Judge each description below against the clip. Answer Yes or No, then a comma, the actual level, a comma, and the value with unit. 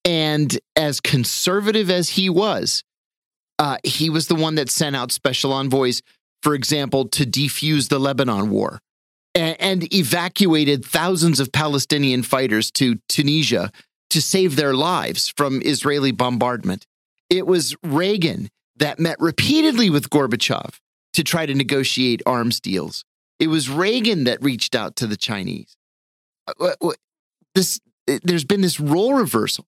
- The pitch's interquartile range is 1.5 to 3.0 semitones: No, average, 4.3 semitones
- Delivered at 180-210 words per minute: No, slow, 135 wpm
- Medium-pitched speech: Yes, medium, 150 Hz